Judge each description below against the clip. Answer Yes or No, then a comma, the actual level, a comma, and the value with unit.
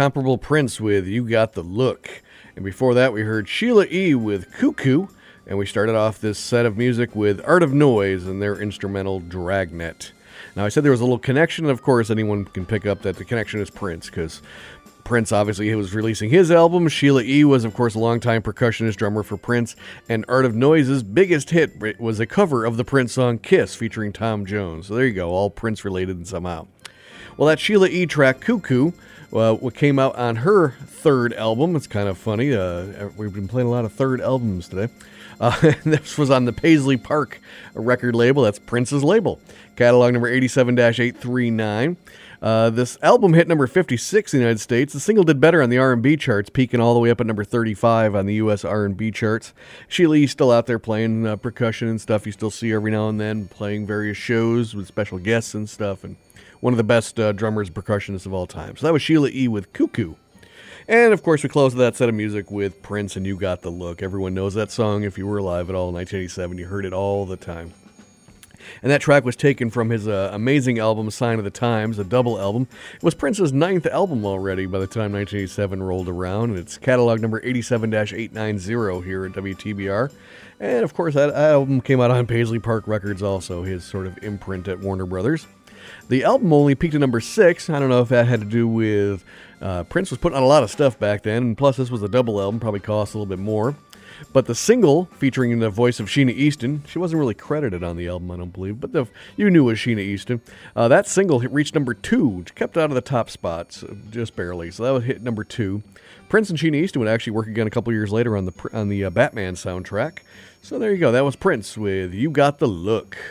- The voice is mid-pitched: No, low, 115 Hz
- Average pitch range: Yes, average, 4.6 semitones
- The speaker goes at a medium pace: No, fast, 220 wpm